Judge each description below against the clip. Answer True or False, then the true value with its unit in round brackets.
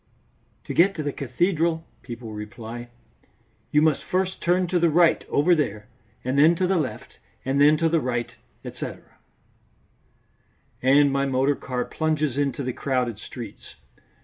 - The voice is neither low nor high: True (145 Hz)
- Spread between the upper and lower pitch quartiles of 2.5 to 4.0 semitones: False (4.6 semitones)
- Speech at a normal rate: True (150 wpm)